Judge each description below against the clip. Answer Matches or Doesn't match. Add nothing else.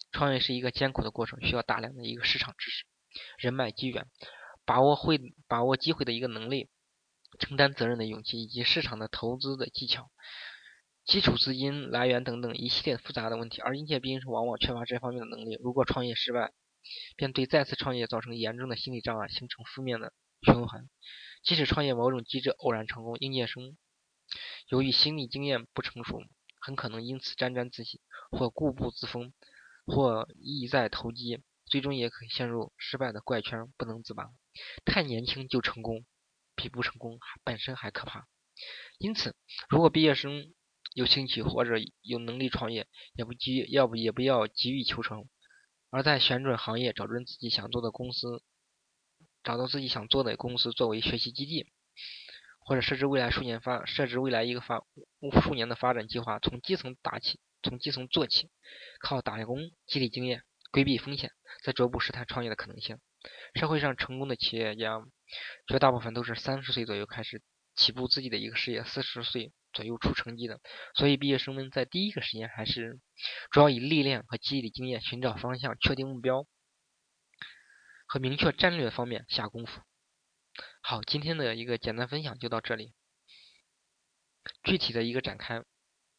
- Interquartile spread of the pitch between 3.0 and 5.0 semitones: Doesn't match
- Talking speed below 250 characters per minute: Doesn't match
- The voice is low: Matches